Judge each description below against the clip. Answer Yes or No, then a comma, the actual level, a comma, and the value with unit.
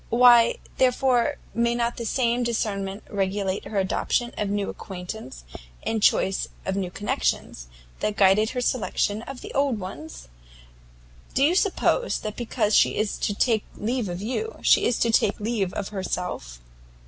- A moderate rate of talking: Yes, average, 155 wpm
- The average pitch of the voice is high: Yes, high, 215 Hz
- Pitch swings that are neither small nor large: Yes, average, 3.7 semitones